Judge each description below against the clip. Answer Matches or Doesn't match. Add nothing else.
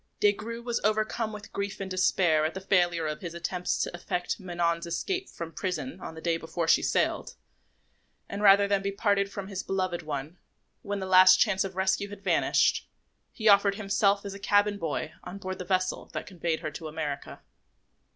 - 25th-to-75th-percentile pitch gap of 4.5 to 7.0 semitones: Doesn't match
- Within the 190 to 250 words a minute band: Matches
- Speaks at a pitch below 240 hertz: Matches